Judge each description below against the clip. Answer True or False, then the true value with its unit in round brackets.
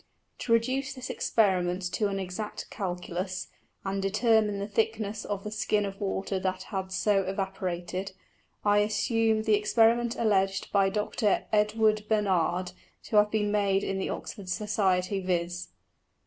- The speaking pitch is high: True (200 Hz)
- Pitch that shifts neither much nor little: False (2.2 semitones)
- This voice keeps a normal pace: True (145 wpm)